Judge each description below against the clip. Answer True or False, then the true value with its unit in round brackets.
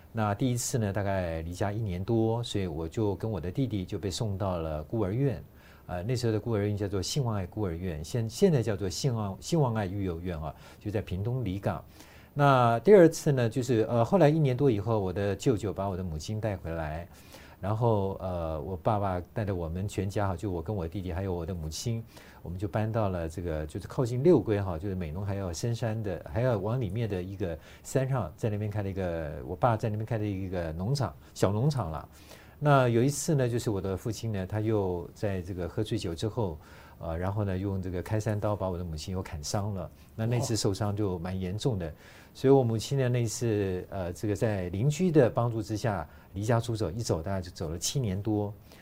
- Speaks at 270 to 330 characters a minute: True (315 characters per minute)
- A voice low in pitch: True (105 Hz)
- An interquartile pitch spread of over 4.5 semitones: False (4.2 semitones)